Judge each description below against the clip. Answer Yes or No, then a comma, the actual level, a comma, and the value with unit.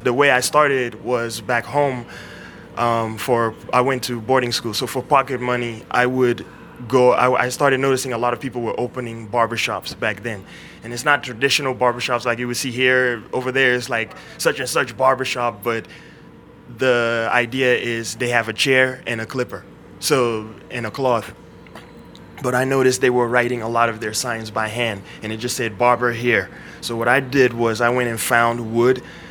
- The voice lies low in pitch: Yes, low, 120 Hz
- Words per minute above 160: Yes, average, 195 wpm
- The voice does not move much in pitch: Yes, narrow, 1.7 semitones